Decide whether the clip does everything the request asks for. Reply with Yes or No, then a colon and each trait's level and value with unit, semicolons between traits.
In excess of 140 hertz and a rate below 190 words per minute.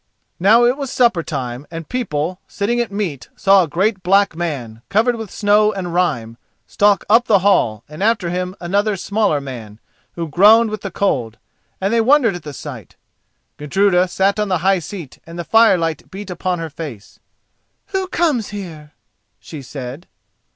Yes: medium, 185 Hz; average, 170 wpm